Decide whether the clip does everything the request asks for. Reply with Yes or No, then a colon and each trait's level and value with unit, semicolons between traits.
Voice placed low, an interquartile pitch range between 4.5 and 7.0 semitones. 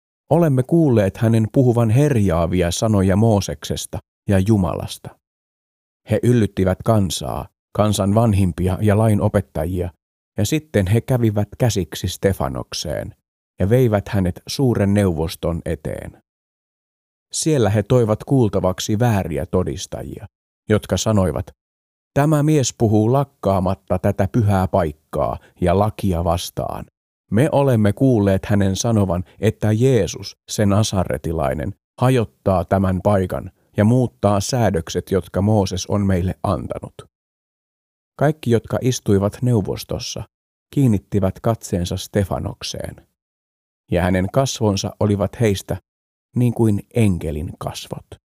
No: low, 100 Hz; average, 4.0 semitones